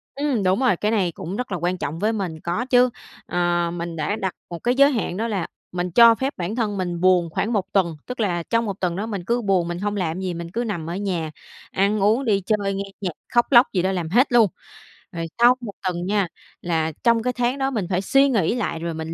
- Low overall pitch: No, high, 195 Hz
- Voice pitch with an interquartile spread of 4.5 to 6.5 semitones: Yes, average, 4.9 semitones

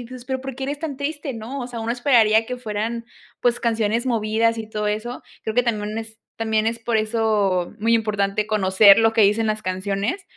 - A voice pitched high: Yes, high, 225 Hz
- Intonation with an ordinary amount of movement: No, narrow, 2.2 semitones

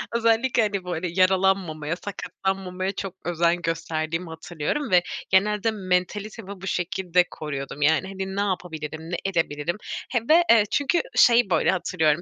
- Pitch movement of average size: Yes, average, 3.4 semitones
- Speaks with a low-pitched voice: No, medium, 185 Hz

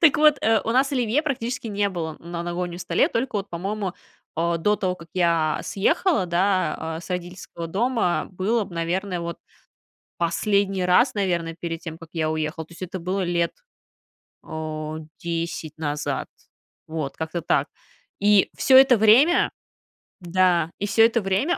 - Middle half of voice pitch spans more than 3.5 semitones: Yes, average, 3.9 semitones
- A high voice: No, medium, 180 Hz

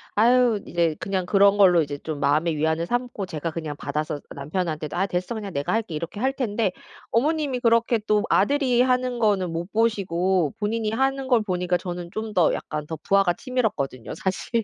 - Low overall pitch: No, high, 195 Hz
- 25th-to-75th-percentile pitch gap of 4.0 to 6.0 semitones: Yes, wide, 5.6 semitones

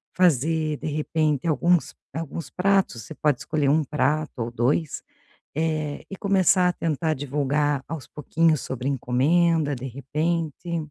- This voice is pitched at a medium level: Yes, medium, 155 Hz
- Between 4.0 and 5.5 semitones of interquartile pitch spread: No, average, 3.0 semitones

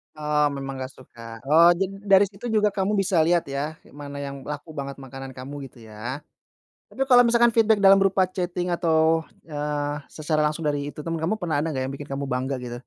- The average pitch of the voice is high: No, medium, 150 Hz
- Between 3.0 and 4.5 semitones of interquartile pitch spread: No, average, 5.2 semitones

